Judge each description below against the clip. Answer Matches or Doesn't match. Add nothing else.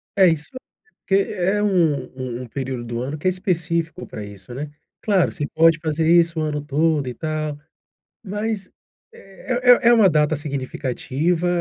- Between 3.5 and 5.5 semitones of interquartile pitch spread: Matches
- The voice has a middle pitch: Matches